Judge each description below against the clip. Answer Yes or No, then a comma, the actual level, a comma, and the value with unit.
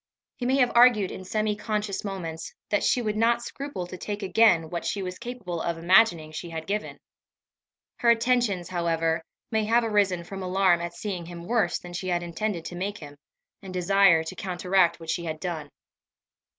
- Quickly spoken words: No, average, 190 wpm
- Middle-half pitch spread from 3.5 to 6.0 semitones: Yes, average, 3.8 semitones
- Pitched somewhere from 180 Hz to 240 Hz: Yes, medium, 185 Hz